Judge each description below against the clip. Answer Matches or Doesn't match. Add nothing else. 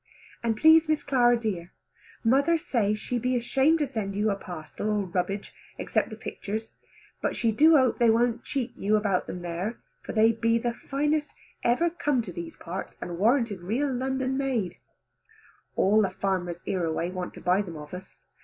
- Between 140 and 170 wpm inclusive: Doesn't match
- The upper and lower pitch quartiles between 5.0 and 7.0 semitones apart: Matches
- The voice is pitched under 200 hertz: Doesn't match